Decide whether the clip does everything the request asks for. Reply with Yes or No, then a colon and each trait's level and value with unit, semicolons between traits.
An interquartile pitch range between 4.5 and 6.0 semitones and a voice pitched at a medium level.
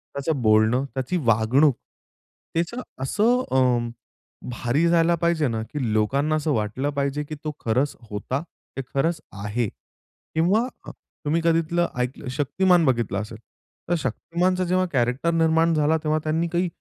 Yes: average, 5.2 semitones; medium, 150 Hz